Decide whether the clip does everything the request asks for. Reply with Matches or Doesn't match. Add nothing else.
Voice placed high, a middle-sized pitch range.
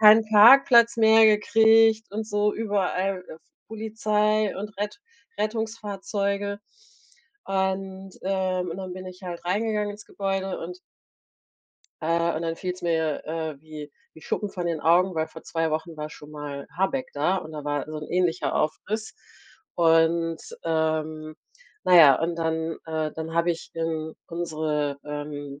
Doesn't match